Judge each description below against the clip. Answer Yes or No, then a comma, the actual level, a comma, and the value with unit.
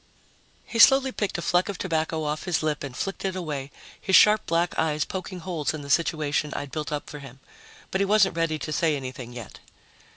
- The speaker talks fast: Yes, fast, 215 wpm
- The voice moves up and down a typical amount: Yes, average, 4.1 semitones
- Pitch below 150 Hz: No, medium, 160 Hz